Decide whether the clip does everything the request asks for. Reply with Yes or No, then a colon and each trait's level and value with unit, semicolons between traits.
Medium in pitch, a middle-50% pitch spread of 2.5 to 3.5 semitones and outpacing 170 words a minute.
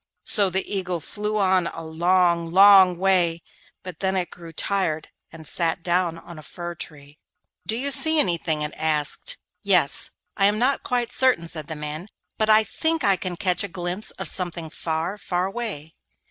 Yes: medium, 180 Hz; average, 3.2 semitones; average, 180 wpm